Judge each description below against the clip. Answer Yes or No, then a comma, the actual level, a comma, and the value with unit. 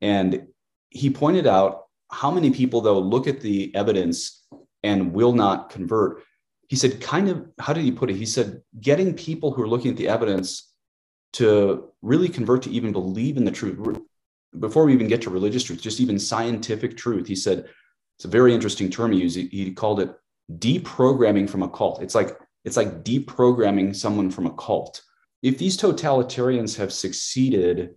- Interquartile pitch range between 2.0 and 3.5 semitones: No, average, 4.9 semitones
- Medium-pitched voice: No, low, 115 Hz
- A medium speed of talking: Yes, average, 180 wpm